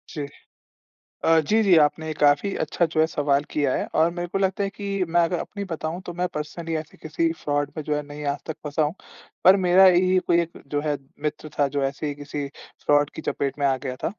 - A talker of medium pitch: Yes, medium, 155 Hz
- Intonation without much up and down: No, average, 3.1 semitones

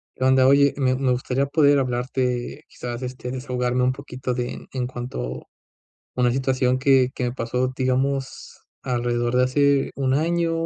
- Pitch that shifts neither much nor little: No, narrow, 1.4 semitones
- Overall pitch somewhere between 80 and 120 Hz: No, low, 130 Hz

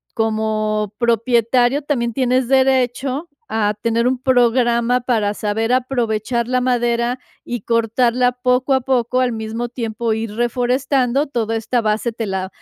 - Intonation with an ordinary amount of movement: No, narrow, 2.1 semitones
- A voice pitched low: No, high, 240 Hz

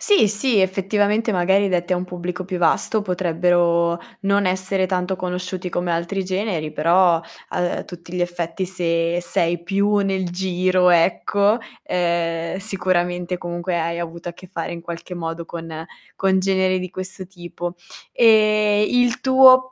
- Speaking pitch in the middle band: Yes, medium, 180 Hz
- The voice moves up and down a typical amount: No, narrow, 2.1 semitones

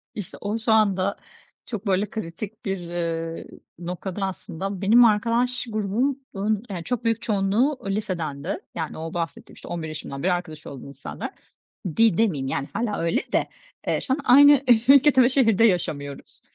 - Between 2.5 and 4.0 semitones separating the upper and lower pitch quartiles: No, average, 5.3 semitones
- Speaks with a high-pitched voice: Yes, high, 195 Hz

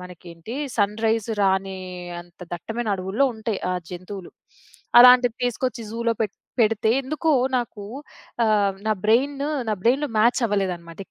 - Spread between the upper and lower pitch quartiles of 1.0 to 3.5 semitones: No, average, 3.9 semitones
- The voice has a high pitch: Yes, high, 220 Hz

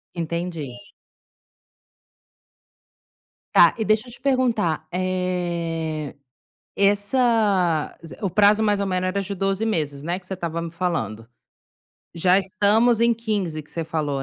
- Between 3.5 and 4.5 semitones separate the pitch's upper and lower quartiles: Yes, average, 4.0 semitones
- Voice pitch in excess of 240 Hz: No, medium, 185 Hz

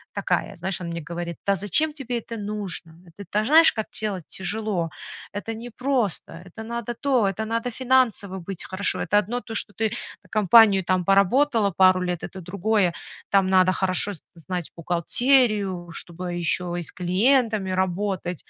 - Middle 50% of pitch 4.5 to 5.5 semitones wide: No, average, 3.8 semitones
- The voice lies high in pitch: Yes, high, 200 Hz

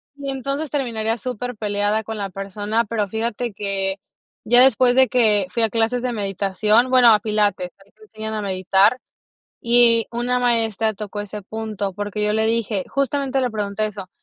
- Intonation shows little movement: No, average, 3.0 semitones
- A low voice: No, high, 220 Hz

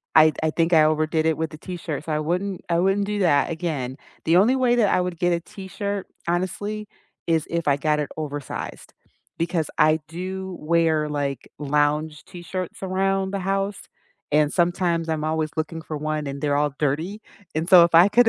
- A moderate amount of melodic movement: Yes, average, 3.5 semitones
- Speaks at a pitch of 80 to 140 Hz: No, medium, 165 Hz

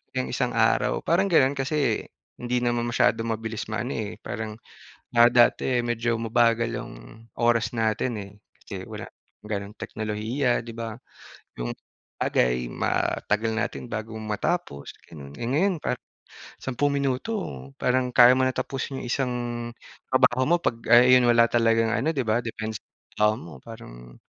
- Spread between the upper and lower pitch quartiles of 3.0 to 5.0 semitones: No, narrow, 2.6 semitones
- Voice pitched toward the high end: No, low, 120 Hz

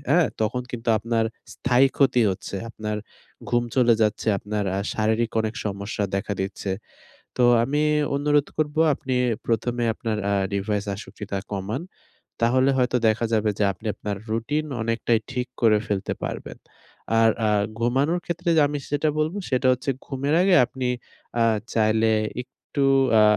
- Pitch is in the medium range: No, low, 115 Hz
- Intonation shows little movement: No, average, 3.8 semitones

